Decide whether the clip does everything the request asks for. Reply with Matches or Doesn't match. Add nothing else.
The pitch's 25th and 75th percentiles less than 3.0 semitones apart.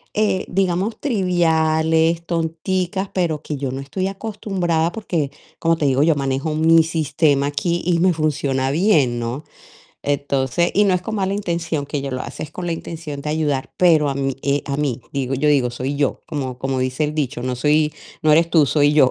Doesn't match